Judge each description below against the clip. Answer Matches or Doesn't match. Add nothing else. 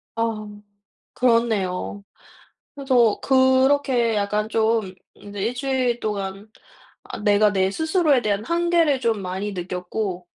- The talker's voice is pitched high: Matches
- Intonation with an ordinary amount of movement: Matches